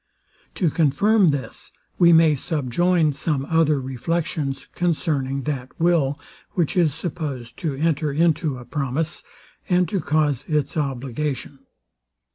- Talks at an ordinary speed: No, slow, 120 wpm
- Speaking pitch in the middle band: Yes, medium, 150 Hz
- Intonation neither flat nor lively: Yes, average, 3.4 semitones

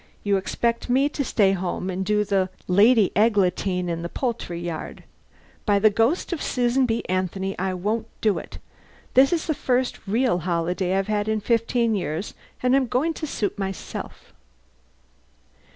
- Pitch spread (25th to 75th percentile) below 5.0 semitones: Yes, average, 4.4 semitones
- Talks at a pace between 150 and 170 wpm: Yes, average, 165 wpm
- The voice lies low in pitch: No, high, 210 Hz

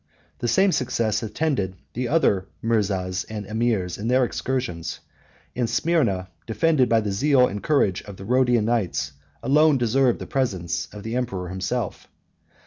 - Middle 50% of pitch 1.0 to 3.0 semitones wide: No, average, 4.9 semitones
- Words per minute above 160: No, average, 150 wpm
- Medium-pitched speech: No, low, 115 Hz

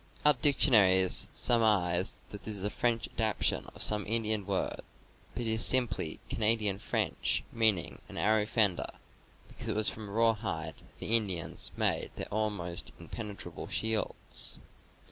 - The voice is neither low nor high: No, low, 105 Hz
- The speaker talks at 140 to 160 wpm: Yes, average, 150 wpm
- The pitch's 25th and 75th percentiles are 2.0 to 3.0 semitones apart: Yes, narrow, 2.6 semitones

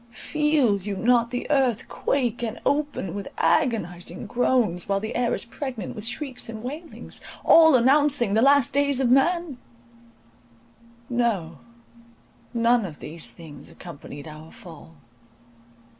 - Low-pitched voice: No, high, 235 Hz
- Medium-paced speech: No, slow, 130 wpm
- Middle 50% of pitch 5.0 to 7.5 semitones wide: Yes, wide, 5.6 semitones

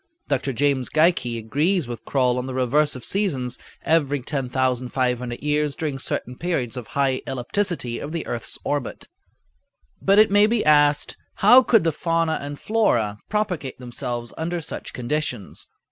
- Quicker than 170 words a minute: No, average, 150 wpm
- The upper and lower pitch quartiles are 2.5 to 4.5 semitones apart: No, average, 4.9 semitones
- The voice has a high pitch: No, medium, 140 Hz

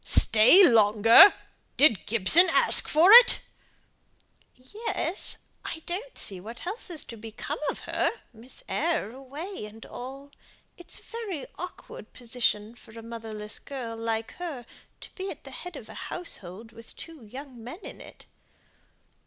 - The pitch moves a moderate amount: No, wide, 7.4 semitones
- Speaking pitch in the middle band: No, very high, 255 Hz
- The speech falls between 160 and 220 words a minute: No, average, 150 wpm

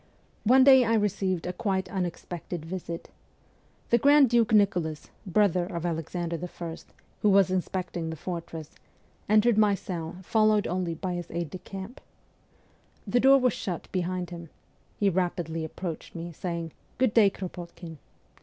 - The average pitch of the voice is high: No, medium, 180 Hz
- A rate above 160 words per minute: No, average, 150 wpm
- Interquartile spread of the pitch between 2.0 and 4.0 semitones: Yes, average, 3.6 semitones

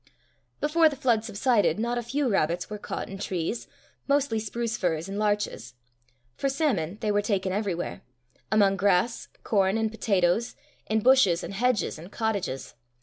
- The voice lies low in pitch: No, high, 210 Hz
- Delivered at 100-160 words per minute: Yes, average, 155 wpm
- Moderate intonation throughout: Yes, average, 3.7 semitones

